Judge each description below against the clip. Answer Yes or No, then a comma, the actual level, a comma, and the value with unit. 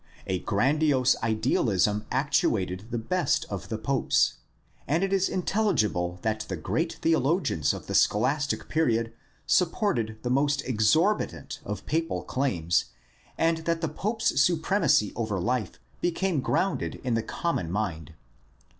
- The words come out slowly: Yes, slow, 130 wpm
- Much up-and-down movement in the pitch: Yes, wide, 7.4 semitones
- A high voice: No, low, 130 Hz